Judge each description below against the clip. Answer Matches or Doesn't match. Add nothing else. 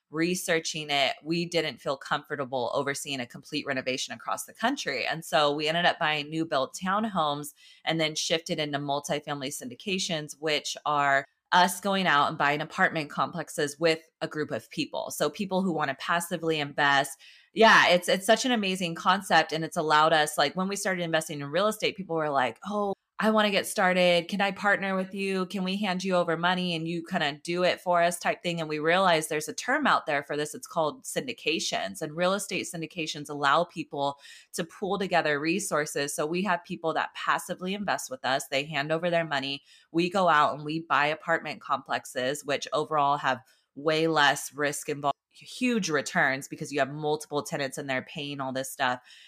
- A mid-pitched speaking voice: Matches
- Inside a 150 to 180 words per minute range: Doesn't match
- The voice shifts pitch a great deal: Doesn't match